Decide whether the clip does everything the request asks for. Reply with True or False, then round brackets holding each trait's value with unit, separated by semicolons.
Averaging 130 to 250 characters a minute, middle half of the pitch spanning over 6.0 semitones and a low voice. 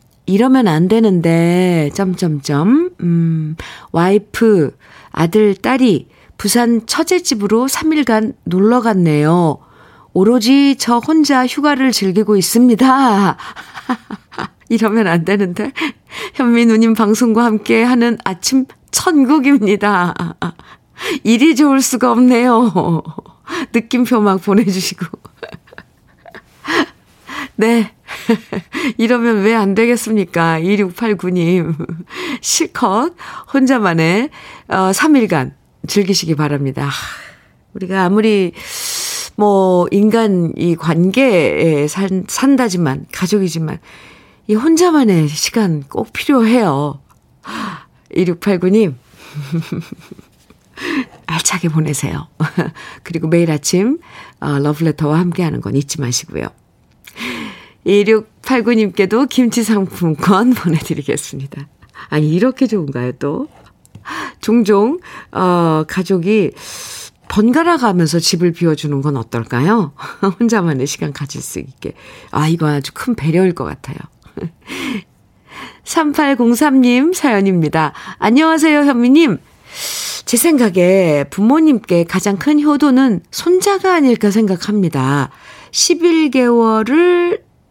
False (205 characters per minute; 6.8 semitones; 205 Hz)